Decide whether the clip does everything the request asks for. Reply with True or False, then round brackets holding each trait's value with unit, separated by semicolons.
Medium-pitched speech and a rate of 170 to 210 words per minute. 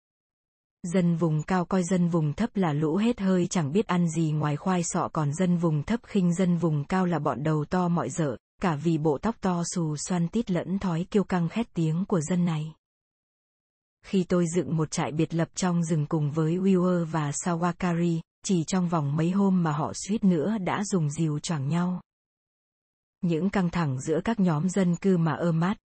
True (175 Hz; 205 wpm)